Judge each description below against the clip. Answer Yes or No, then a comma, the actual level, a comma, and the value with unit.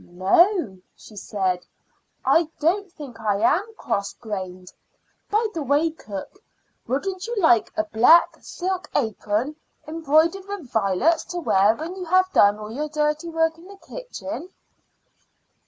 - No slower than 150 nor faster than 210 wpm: No, average, 140 wpm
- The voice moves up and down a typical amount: No, wide, 8.7 semitones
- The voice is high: Yes, very high, 305 Hz